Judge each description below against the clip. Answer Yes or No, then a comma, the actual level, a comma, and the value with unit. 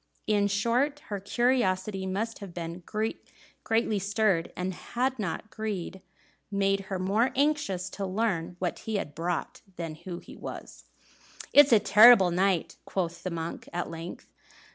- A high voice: Yes, high, 195 Hz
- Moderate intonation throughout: Yes, average, 3.8 semitones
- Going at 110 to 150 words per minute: Yes, average, 140 wpm